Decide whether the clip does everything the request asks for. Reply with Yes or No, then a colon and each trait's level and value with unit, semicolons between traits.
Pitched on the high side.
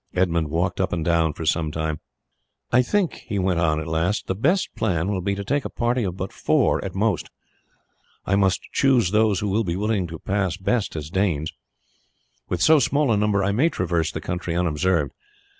No: very low, 95 Hz